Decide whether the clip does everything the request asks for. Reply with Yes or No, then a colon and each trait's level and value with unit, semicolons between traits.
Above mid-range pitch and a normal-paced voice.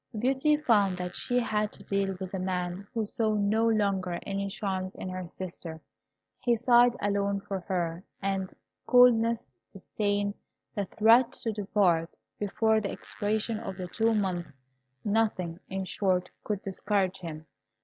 Yes: high, 200 Hz; average, 150 wpm